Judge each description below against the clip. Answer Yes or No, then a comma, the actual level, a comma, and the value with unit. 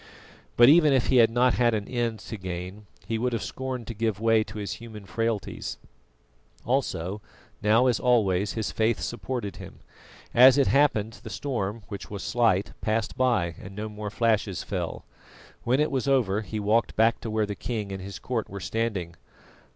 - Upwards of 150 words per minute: Yes, average, 185 wpm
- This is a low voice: Yes, low, 110 Hz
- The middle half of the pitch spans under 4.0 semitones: Yes, average, 2.9 semitones